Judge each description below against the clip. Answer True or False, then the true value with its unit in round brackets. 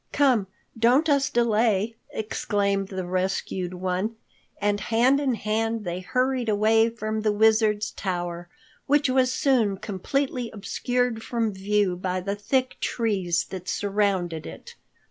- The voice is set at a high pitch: True (215 Hz)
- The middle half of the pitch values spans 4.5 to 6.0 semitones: False (3.8 semitones)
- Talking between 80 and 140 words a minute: True (135 wpm)